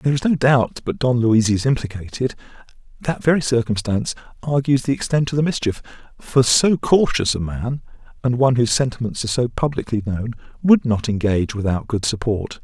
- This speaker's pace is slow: No, average, 175 wpm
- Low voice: Yes, low, 125 Hz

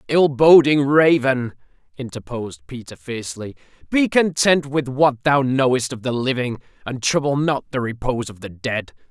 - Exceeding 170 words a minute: No, average, 150 wpm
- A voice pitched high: No, low, 130 Hz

